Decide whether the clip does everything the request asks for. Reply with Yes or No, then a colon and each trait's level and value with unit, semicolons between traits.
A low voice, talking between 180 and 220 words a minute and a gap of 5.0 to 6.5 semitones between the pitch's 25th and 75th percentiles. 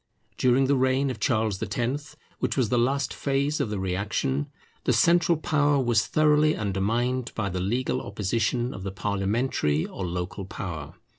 No: low, 120 Hz; average, 160 wpm; wide, 5.6 semitones